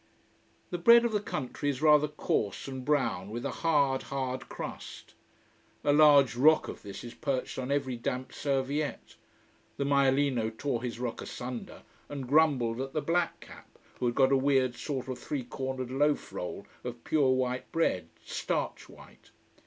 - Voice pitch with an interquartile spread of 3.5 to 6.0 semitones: No, narrow, 2.6 semitones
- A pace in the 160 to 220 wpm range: Yes, average, 170 wpm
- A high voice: No, low, 135 Hz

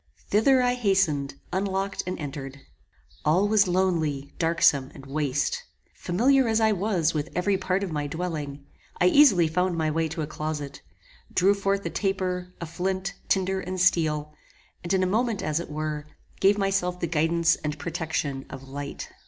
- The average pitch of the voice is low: No, medium, 175 Hz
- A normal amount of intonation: Yes, average, 4.2 semitones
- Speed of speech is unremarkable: Yes, average, 170 wpm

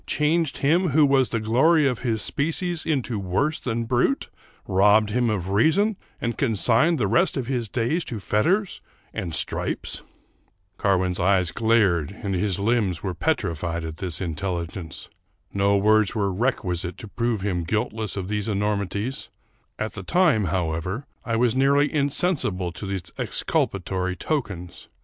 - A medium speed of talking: Yes, average, 160 wpm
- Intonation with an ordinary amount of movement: No, wide, 6.1 semitones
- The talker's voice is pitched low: Yes, low, 105 Hz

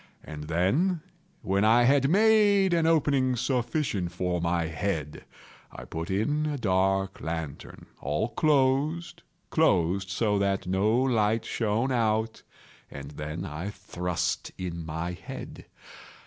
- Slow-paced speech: Yes, slow, 120 wpm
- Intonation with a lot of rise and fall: Yes, wide, 7.5 semitones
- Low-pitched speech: Yes, low, 105 Hz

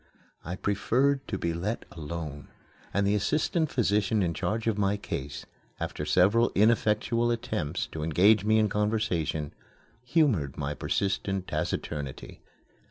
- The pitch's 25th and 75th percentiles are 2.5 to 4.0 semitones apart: No, average, 5.0 semitones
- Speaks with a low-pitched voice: Yes, low, 100 Hz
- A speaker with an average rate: No, slow, 130 wpm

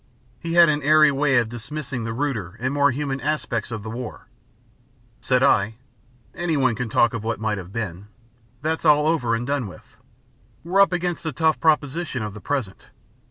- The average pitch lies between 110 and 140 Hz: Yes, low, 135 Hz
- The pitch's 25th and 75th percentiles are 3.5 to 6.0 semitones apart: Yes, average, 5.1 semitones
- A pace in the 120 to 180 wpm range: No, average, 190 wpm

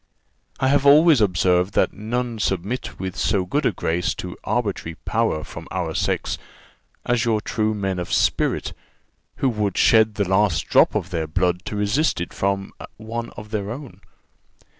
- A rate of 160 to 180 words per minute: Yes, average, 165 wpm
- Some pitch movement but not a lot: Yes, average, 4.1 semitones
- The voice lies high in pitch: No, low, 105 Hz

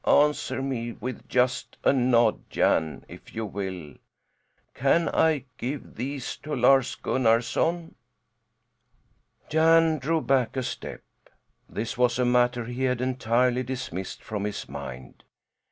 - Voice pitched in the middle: No, low, 125 Hz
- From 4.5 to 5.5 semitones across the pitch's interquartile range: No, average, 2.9 semitones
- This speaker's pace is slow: Yes, slow, 125 wpm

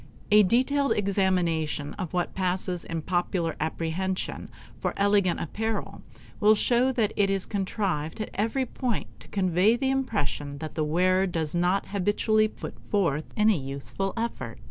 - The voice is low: No, high, 190 Hz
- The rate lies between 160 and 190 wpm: No, average, 145 wpm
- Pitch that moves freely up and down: No, average, 4.2 semitones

